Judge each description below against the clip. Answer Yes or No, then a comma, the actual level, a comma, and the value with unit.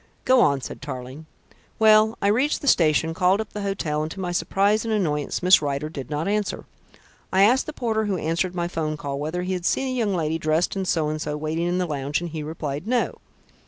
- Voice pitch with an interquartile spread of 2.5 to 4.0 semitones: No, average, 4.9 semitones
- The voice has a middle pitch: Yes, medium, 175 Hz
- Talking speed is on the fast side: Yes, fast, 230 wpm